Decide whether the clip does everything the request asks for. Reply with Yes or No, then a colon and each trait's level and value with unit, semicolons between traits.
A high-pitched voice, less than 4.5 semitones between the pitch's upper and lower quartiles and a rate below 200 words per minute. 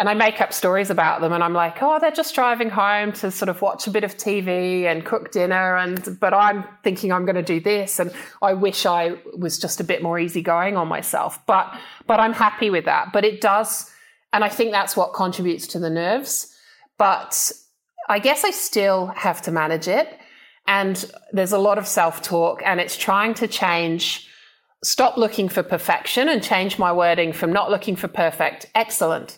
No: high, 195 Hz; average, 3.4 semitones; fast, 205 wpm